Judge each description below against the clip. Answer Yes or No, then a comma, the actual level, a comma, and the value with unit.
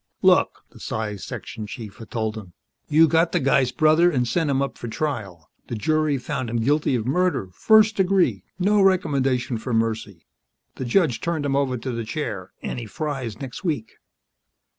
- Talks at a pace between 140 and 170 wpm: No, average, 185 wpm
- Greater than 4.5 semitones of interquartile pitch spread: Yes, wide, 5.6 semitones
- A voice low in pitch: Yes, low, 130 Hz